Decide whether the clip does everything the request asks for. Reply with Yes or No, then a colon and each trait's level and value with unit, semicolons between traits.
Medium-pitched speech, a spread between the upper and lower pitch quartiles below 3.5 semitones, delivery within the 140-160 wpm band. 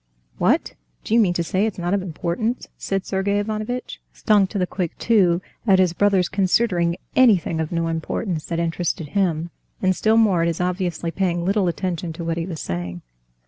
No: medium, 180 Hz; average, 3.0 semitones; average, 190 wpm